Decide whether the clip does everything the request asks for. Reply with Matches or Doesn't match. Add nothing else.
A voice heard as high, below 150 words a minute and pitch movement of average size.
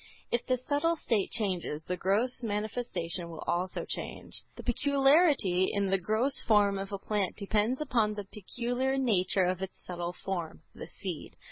Doesn't match